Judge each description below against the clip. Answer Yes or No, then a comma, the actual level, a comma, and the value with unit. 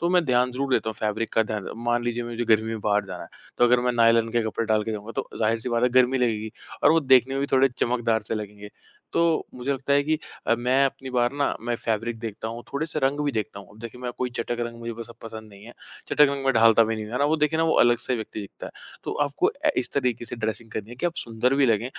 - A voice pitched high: No, low, 120 Hz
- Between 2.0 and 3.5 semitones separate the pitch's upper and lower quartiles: Yes, average, 2.9 semitones